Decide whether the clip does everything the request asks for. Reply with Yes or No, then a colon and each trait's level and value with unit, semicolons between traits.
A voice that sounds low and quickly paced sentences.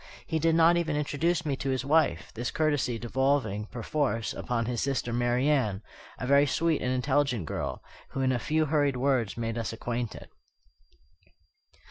No: low, 130 Hz; average, 160 wpm